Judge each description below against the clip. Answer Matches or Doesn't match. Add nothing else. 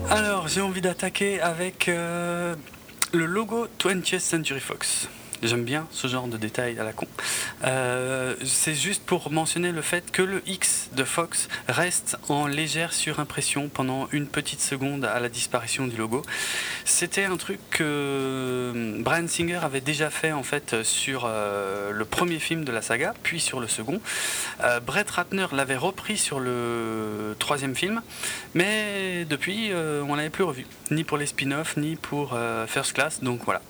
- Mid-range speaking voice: Matches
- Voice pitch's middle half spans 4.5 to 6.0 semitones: Matches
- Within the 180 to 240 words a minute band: Doesn't match